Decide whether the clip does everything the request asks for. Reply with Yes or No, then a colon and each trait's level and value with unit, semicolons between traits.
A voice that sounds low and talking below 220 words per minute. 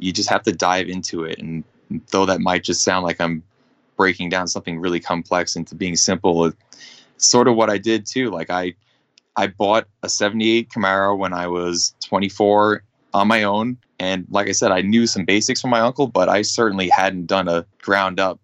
Yes: very low, 95 Hz; fast, 205 wpm